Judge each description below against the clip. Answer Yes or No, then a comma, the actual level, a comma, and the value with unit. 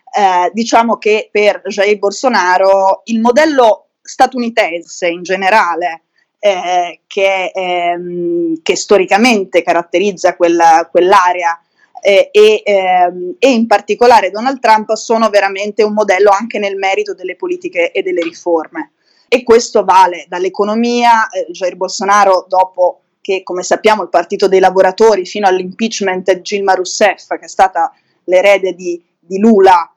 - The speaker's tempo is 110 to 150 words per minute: Yes, average, 130 wpm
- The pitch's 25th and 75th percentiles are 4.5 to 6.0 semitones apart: No, average, 3.8 semitones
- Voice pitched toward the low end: No, high, 195 Hz